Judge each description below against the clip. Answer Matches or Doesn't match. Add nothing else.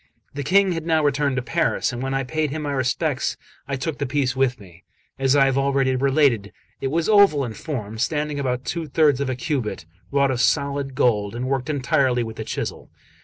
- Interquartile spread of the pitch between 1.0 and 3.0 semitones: Matches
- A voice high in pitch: Doesn't match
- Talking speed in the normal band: Doesn't match